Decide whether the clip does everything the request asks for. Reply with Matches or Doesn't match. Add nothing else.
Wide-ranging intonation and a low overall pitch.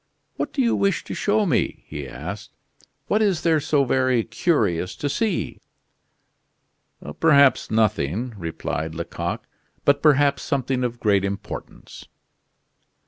Matches